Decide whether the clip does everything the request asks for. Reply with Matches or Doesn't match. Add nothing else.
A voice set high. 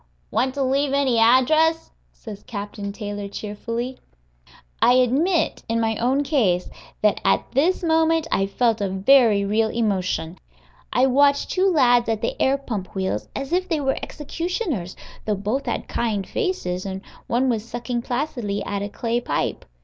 Matches